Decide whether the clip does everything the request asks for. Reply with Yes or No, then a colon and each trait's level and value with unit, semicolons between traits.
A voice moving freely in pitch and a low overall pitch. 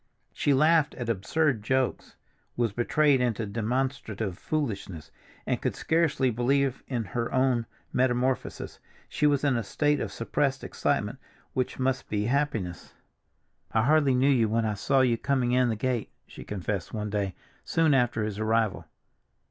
No: average, 3.8 semitones; low, 125 Hz